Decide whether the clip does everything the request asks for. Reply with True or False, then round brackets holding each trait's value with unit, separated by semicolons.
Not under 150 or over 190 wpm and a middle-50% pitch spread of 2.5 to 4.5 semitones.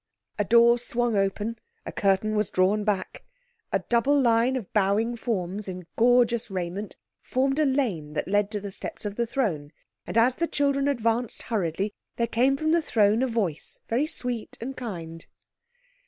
True (170 wpm; 3.7 semitones)